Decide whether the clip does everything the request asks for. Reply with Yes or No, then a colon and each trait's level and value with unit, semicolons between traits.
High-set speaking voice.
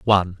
No: very low, 95 Hz